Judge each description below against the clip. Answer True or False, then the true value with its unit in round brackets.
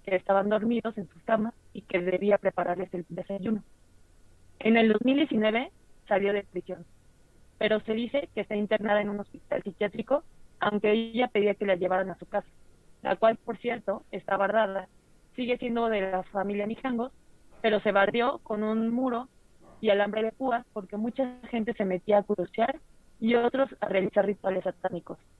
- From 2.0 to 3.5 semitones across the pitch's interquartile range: True (3.1 semitones)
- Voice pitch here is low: False (210 Hz)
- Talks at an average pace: True (170 wpm)